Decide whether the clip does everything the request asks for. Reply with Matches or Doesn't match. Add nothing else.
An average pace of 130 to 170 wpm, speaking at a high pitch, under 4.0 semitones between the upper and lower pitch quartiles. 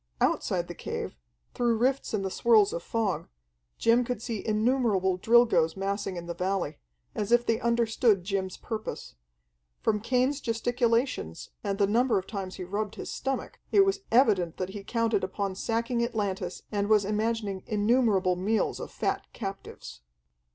Matches